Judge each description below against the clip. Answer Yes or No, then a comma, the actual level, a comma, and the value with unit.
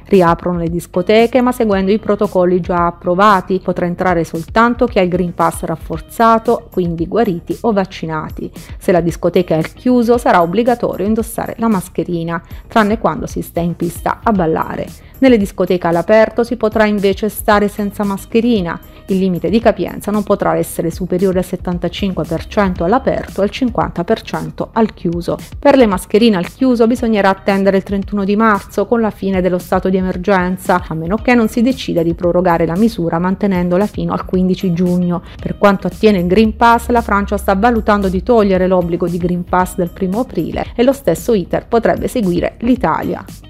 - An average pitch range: Yes, average, 3.7 semitones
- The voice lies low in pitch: No, high, 195 Hz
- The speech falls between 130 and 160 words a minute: No, fast, 170 wpm